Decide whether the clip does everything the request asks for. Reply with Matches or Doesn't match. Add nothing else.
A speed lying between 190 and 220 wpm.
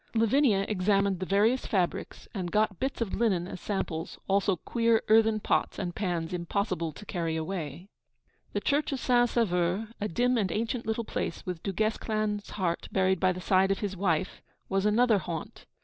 Doesn't match